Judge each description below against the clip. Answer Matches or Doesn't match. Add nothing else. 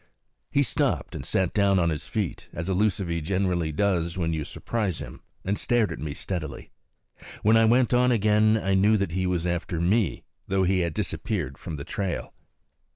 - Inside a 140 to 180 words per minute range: Doesn't match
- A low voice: Matches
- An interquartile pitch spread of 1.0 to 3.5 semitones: Doesn't match